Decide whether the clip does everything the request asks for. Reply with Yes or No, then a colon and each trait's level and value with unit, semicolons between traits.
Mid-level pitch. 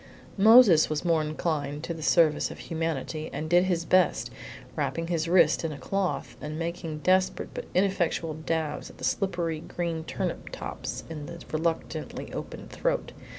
Yes: medium, 165 Hz